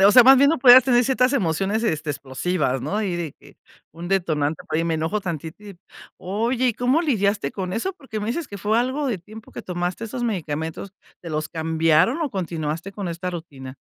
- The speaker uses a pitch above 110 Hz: Yes, high, 190 Hz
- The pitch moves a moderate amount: No, wide, 6.5 semitones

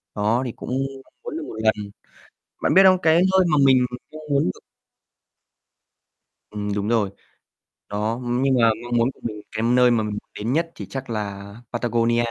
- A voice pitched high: No, low, 120 Hz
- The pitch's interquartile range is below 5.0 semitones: Yes, average, 4.1 semitones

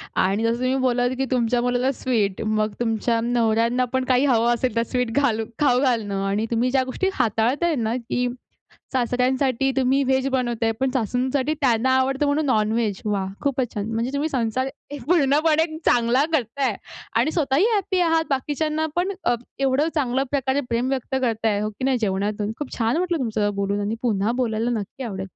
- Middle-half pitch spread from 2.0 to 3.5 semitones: Yes, average, 3.2 semitones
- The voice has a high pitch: Yes, very high, 250 Hz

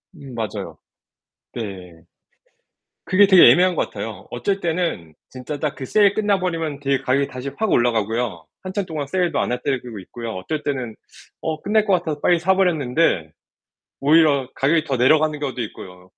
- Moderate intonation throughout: No, wide, 6.0 semitones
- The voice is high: No, medium, 145 Hz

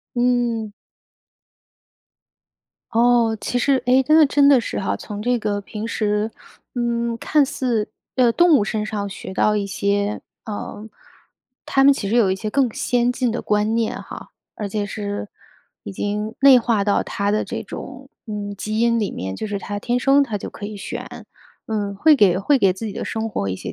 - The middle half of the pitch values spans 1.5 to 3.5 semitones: Yes, average, 3.2 semitones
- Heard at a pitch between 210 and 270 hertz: Yes, high, 220 Hz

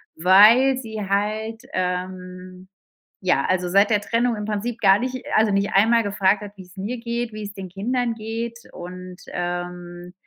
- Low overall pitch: No, high, 205 Hz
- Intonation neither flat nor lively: Yes, average, 3.7 semitones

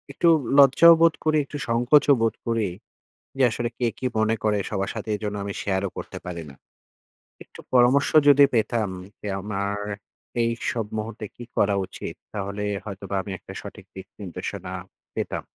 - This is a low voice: Yes, low, 110 Hz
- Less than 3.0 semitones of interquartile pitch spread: No, average, 3.5 semitones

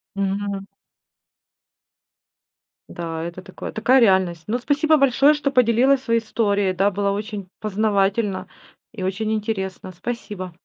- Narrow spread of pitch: No, average, 3.4 semitones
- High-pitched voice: Yes, high, 205 Hz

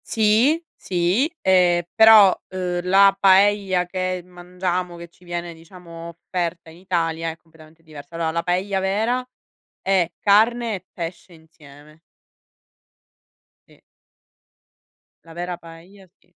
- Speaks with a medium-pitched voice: Yes, medium, 180 Hz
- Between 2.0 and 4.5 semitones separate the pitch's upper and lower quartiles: Yes, narrow, 2.5 semitones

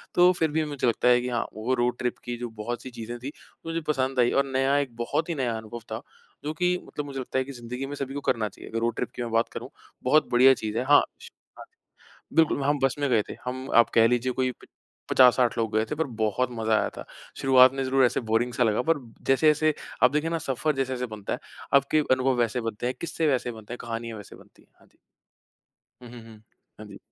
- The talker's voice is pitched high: No, low, 125 Hz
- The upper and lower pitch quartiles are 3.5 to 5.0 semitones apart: No, average, 2.9 semitones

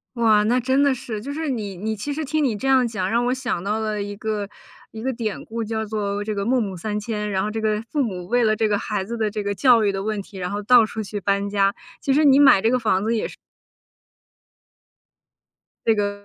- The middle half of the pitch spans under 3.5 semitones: Yes, average, 3.0 semitones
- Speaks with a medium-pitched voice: No, high, 220 Hz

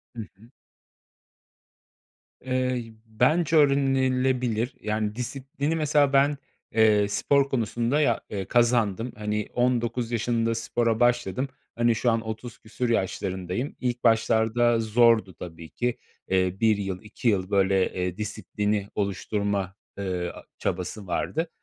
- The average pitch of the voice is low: Yes, low, 115 Hz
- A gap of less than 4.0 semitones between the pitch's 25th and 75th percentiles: Yes, average, 3.4 semitones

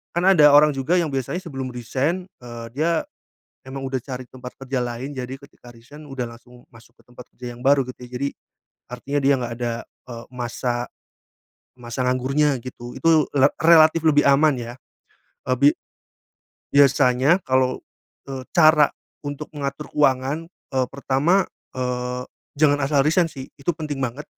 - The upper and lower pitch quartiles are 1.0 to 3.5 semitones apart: Yes, average, 2.9 semitones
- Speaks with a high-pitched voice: No, low, 135 Hz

